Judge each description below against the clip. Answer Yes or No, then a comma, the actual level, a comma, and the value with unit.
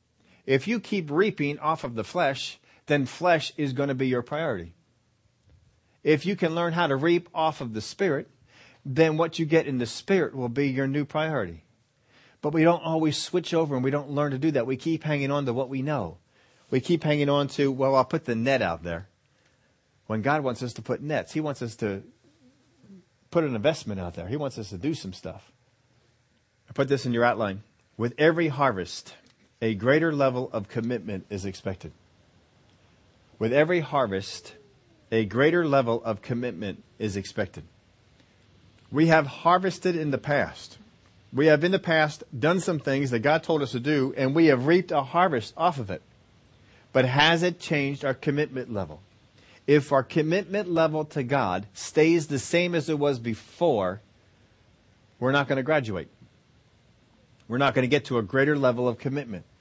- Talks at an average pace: Yes, average, 185 wpm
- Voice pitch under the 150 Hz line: Yes, low, 135 Hz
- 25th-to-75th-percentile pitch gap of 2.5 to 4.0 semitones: No, wide, 5.5 semitones